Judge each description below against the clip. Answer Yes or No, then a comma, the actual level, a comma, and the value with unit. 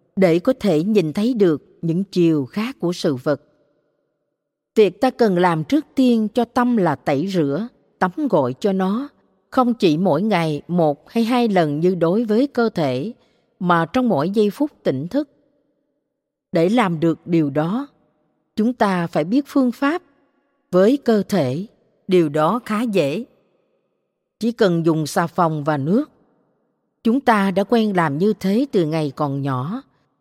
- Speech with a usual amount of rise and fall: No, wide, 6.8 semitones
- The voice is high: Yes, high, 200 Hz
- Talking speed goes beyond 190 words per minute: No, slow, 165 wpm